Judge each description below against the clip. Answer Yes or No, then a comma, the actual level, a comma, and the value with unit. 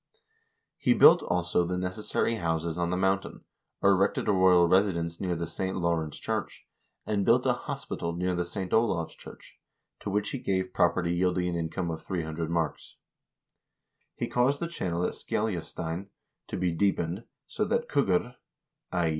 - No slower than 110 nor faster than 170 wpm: Yes, average, 165 wpm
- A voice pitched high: No, very low, 90 Hz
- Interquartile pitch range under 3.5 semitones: Yes, narrow, 2.4 semitones